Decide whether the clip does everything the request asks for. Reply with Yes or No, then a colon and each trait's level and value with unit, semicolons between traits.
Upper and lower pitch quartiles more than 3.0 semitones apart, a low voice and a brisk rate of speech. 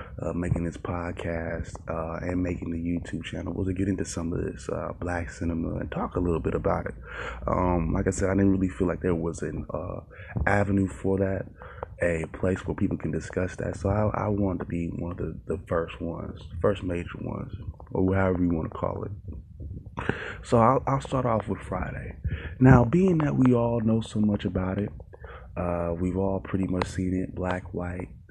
No: average, 2.7 semitones; very low, 95 Hz; fast, 210 wpm